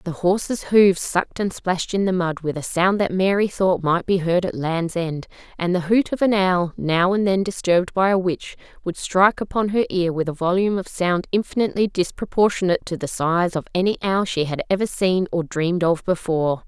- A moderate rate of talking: No, fast, 215 wpm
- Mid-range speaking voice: Yes, medium, 180 Hz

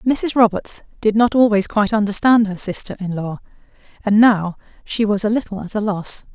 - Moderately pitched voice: No, high, 210 Hz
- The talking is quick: No, average, 190 wpm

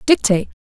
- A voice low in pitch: No, high, 225 Hz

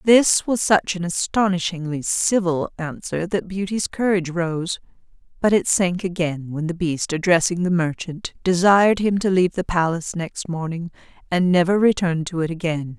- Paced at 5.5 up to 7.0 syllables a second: No, 4.9 syllables/s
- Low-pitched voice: No, medium, 175 Hz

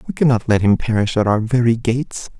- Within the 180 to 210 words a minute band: No, fast, 225 wpm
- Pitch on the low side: Yes, low, 115 Hz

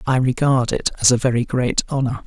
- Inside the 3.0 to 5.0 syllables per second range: No, 5.5 syllables/s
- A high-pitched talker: No, low, 125 Hz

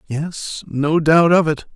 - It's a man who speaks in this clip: Yes, male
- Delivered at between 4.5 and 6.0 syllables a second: No, 3.4 syllables/s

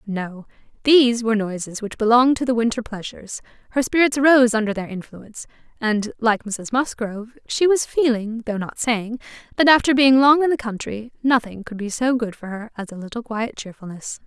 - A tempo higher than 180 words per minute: Yes, average, 190 wpm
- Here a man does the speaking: No, female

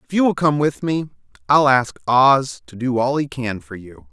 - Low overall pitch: Yes, low, 130 Hz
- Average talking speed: No, fast, 235 wpm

